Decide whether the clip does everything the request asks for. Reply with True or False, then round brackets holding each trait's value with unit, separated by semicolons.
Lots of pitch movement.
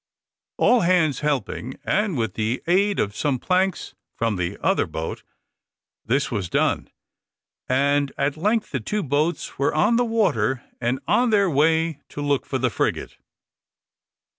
True (6.5 semitones)